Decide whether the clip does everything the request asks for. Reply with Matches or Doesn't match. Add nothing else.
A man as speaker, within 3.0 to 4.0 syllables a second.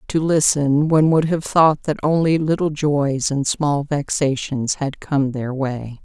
Doesn't match